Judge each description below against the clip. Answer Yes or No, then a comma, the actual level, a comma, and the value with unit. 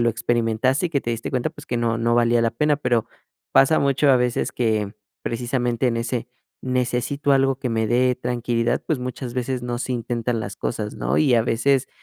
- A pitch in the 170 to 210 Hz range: No, low, 120 Hz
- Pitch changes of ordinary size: No, narrow, 1.9 semitones